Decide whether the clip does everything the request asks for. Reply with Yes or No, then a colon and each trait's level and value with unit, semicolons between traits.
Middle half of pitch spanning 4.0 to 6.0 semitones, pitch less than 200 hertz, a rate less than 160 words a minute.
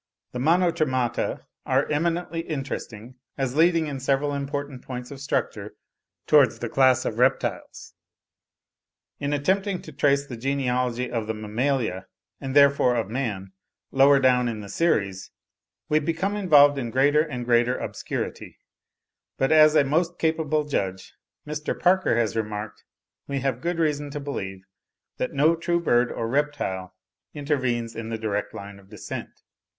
Yes: average, 4.3 semitones; low, 135 Hz; average, 145 wpm